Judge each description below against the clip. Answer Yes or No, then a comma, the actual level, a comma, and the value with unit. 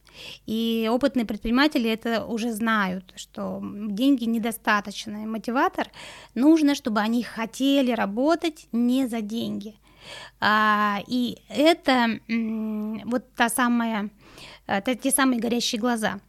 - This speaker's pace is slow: Yes, slow, 100 wpm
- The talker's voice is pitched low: No, high, 230 Hz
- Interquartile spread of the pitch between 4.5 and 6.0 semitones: No, average, 2.8 semitones